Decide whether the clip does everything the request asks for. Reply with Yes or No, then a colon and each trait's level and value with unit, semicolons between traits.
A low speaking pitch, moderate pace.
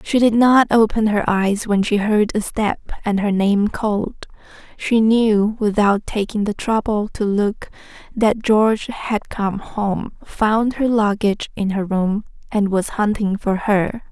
No: high, 210 Hz; average, 165 wpm